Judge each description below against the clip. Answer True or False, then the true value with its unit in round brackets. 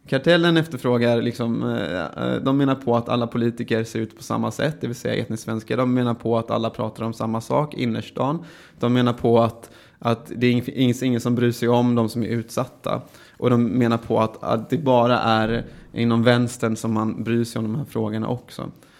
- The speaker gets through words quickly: True (205 wpm)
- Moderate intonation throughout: False (1.4 semitones)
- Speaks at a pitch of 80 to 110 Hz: False (120 Hz)